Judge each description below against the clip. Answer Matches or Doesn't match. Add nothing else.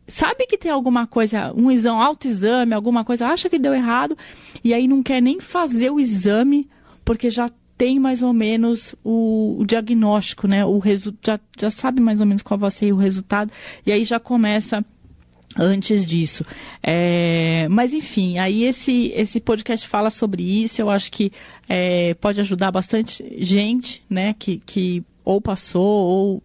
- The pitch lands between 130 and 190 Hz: Doesn't match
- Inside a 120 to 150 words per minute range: Doesn't match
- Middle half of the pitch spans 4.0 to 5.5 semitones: Doesn't match